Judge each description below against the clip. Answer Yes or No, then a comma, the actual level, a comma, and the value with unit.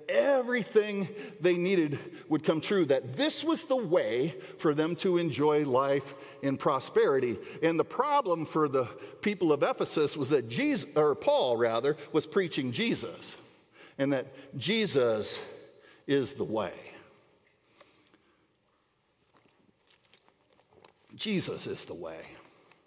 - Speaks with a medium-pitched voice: Yes, medium, 180 Hz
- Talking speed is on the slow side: Yes, slow, 120 wpm